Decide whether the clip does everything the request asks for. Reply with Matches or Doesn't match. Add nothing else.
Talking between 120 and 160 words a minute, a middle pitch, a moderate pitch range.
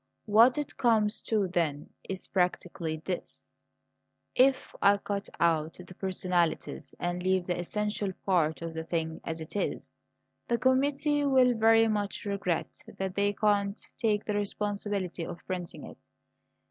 Doesn't match